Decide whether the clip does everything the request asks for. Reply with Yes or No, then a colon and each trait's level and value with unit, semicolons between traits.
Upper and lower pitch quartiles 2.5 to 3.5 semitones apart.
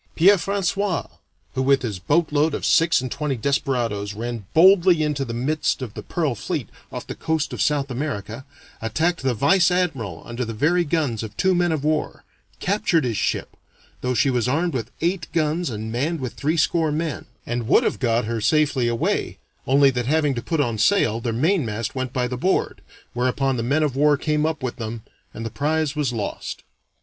No: average, 5.1 semitones